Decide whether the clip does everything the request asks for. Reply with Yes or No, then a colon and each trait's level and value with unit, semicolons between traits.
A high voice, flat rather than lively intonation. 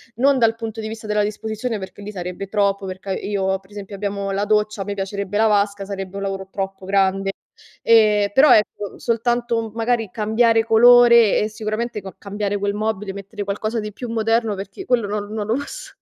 Yes: high, 210 Hz; narrow, 2.1 semitones